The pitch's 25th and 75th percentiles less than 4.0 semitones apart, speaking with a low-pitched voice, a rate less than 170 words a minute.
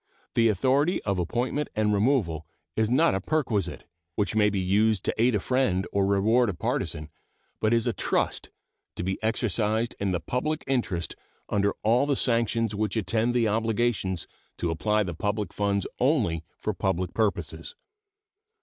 Yes: average, 3.6 semitones; low, 110 Hz; average, 160 wpm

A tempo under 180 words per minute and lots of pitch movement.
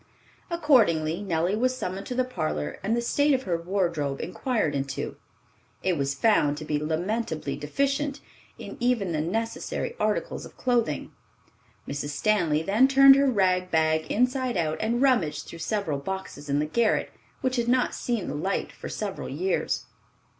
Yes: average, 160 wpm; wide, 8.0 semitones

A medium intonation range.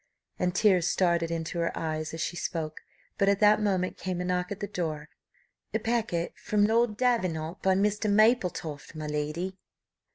Yes: average, 4.0 semitones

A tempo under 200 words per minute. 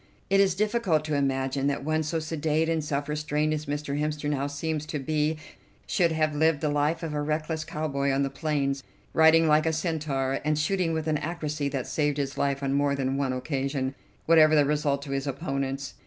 No: fast, 205 wpm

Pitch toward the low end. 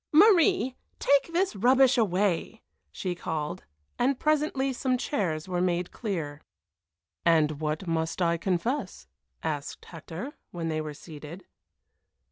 No: medium, 185 Hz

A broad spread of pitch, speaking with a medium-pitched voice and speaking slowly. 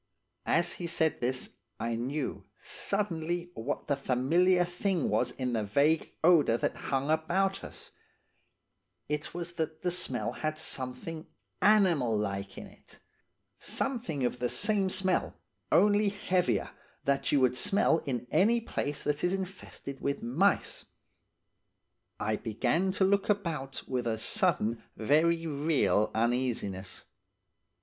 Yes: wide, 6.3 semitones; medium, 155 Hz; slow, 130 wpm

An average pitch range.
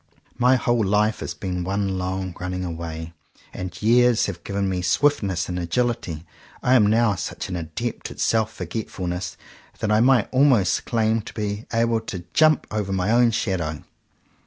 Yes: average, 4.2 semitones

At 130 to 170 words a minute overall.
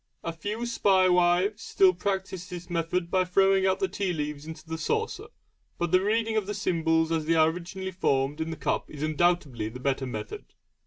No: average, 200 wpm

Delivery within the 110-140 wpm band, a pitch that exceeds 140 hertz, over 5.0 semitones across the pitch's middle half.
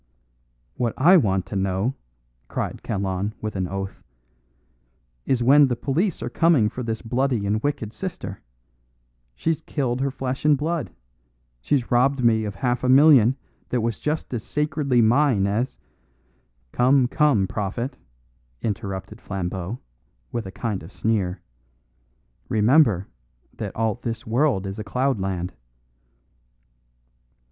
No: slow, 135 wpm; low, 115 Hz; wide, 5.4 semitones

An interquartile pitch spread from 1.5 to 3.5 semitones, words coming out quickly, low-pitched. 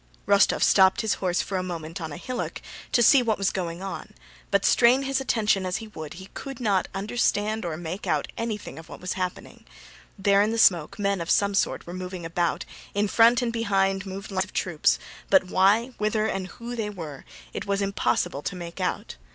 No: average, 3.0 semitones; fast, 210 wpm; high, 195 Hz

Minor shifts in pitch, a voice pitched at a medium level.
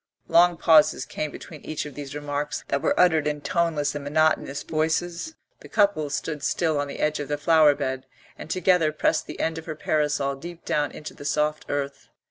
Yes: narrow, 2.0 semitones; medium, 150 Hz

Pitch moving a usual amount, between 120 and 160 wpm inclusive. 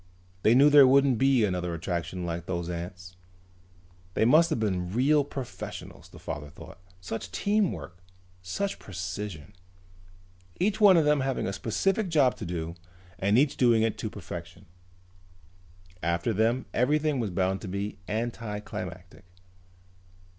No: wide, 7.1 semitones; average, 140 wpm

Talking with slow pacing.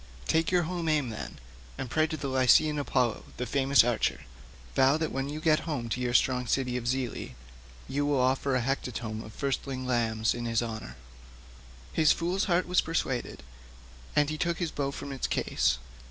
No: average, 185 wpm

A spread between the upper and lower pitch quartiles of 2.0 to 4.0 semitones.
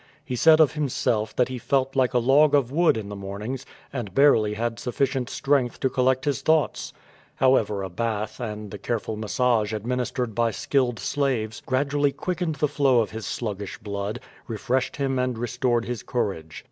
Yes: average, 3.7 semitones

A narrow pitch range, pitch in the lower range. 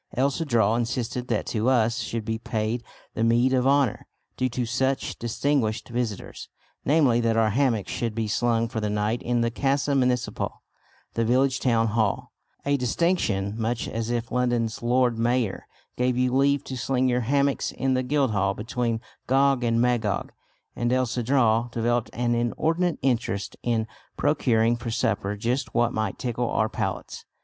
Yes: narrow, 2.2 semitones; low, 120 Hz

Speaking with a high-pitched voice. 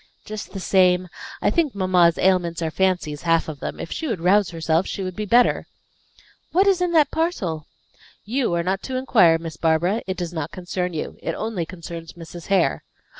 No: medium, 180 Hz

